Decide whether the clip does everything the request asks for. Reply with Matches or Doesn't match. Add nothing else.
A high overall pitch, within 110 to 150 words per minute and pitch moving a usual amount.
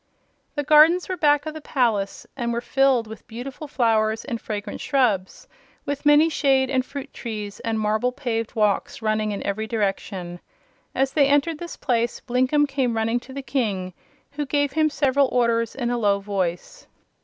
Doesn't match